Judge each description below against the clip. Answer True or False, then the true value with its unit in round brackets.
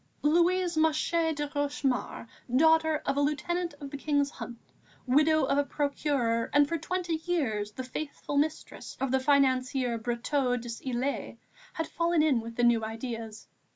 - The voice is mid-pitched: False (285 Hz)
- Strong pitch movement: False (4.2 semitones)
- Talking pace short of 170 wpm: True (155 wpm)